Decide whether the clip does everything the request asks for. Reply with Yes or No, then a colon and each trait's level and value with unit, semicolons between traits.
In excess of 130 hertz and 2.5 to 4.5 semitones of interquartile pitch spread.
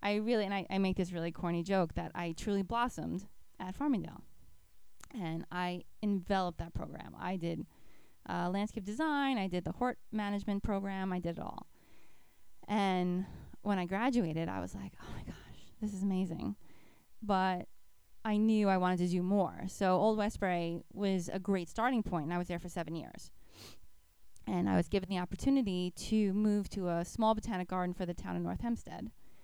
Yes: high, 190 Hz; average, 2.8 semitones